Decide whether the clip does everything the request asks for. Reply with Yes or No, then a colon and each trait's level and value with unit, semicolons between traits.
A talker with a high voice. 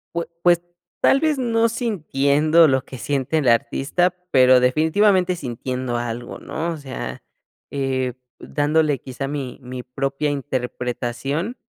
No: medium, 140 Hz